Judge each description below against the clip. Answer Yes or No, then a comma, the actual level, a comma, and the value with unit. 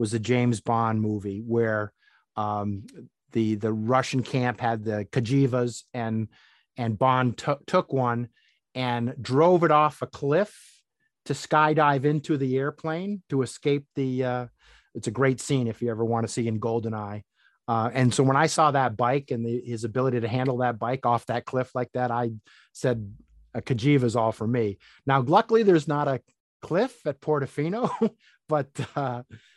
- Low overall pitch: Yes, low, 125 Hz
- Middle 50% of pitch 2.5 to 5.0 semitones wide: Yes, average, 3.4 semitones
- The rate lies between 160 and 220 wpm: Yes, average, 175 wpm